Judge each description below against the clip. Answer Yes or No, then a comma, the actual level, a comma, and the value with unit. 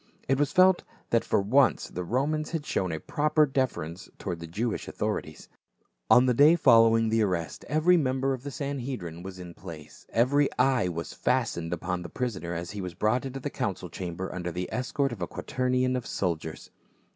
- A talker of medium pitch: No, low, 115 Hz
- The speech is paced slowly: No, average, 190 wpm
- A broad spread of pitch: Yes, wide, 7.2 semitones